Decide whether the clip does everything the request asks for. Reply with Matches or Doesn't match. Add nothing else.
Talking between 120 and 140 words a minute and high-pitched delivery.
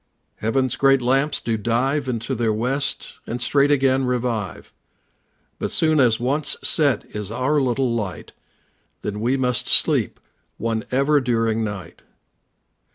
Doesn't match